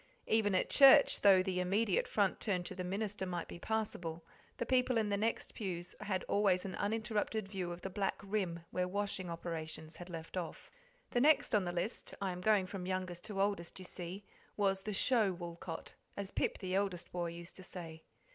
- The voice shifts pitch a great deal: No, average, 2.9 semitones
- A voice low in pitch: No, high, 190 Hz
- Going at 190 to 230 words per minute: Yes, average, 200 wpm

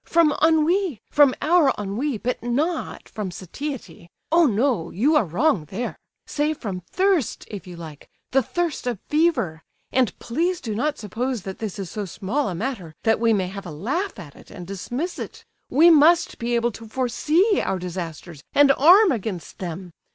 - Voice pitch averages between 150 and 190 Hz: No, high, 240 Hz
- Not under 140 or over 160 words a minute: No, average, 180 wpm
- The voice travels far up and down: Yes, wide, 8.0 semitones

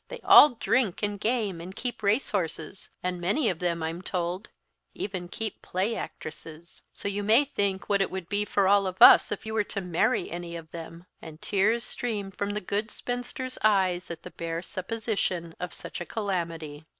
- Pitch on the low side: No, high, 195 Hz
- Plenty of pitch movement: No, average, 3.7 semitones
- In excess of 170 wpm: Yes, average, 195 wpm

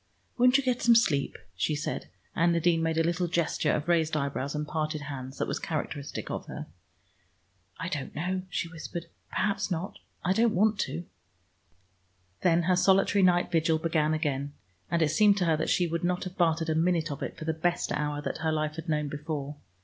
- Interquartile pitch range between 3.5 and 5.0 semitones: No, average, 2.7 semitones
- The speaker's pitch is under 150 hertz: No, medium, 165 Hz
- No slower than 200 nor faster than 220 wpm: Yes, fast, 205 wpm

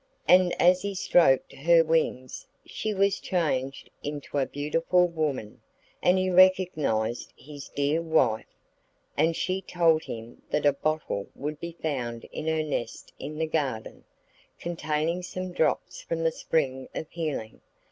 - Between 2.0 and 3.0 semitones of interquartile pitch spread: No, average, 4.0 semitones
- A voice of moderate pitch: Yes, medium, 155 Hz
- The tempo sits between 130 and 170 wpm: Yes, average, 145 wpm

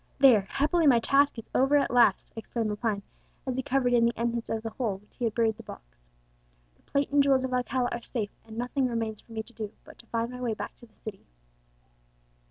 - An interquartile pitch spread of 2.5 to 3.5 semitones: Yes, average, 2.8 semitones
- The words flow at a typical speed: No, fast, 240 wpm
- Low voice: No, high, 235 Hz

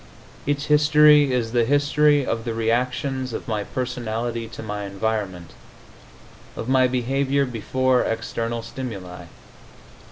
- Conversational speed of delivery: No, slow, 120 wpm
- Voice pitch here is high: No, low, 120 Hz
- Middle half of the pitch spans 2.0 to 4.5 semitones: Yes, average, 3.1 semitones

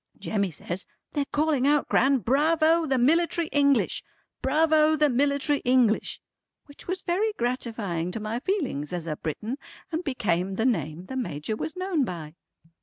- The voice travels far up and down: Yes, wide, 6.7 semitones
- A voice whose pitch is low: No, very high, 265 Hz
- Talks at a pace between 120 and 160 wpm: Yes, average, 155 wpm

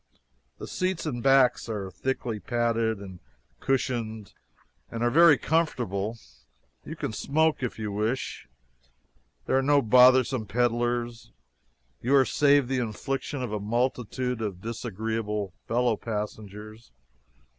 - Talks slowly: Yes, slow, 125 wpm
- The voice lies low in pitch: Yes, low, 120 Hz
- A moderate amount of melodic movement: Yes, average, 3.3 semitones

